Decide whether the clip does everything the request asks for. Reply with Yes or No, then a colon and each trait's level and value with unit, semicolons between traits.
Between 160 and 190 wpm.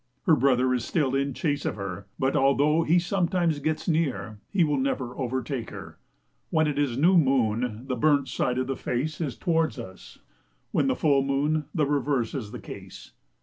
Yes: average, 185 wpm